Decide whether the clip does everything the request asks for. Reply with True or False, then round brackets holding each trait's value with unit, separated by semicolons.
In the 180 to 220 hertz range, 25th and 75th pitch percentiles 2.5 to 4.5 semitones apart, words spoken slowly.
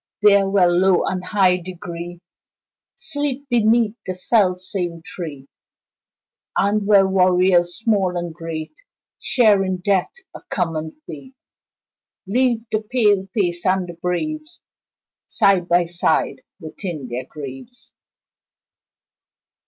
True (185 Hz; 3.4 semitones; 115 wpm)